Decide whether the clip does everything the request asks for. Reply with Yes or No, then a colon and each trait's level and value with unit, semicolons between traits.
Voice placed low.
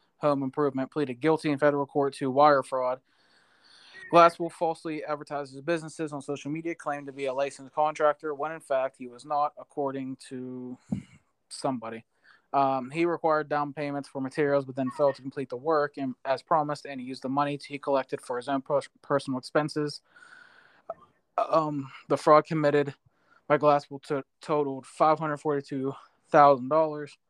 No: medium, 145 Hz